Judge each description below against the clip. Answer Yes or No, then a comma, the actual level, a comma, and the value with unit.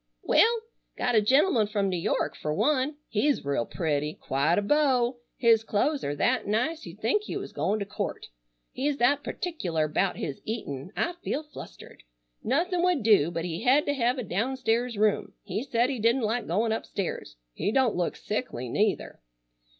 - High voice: Yes, high, 225 Hz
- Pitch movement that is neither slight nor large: No, wide, 6.2 semitones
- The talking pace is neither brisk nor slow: Yes, average, 180 wpm